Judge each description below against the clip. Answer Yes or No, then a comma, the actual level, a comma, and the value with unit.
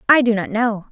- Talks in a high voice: Yes, high, 230 Hz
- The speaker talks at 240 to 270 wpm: Yes, fast, 260 wpm